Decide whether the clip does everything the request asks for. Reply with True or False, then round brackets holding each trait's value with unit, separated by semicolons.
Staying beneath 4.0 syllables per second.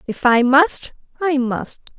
True (3.6 syllables/s)